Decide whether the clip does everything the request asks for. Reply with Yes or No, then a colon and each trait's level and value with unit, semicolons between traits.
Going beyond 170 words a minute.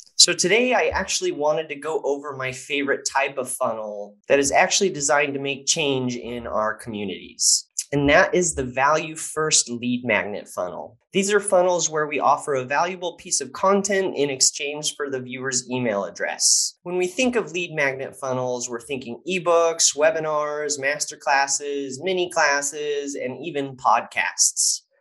No: average, 165 wpm